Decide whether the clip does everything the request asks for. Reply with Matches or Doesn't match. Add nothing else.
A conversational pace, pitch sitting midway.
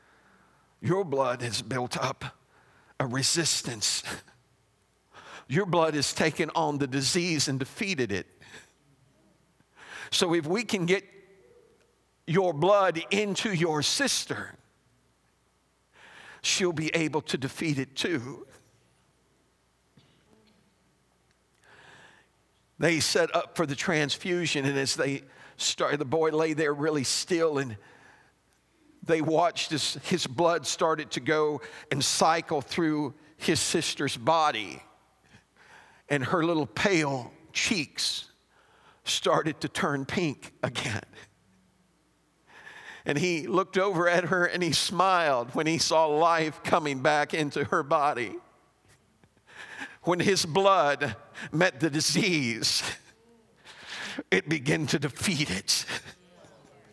Doesn't match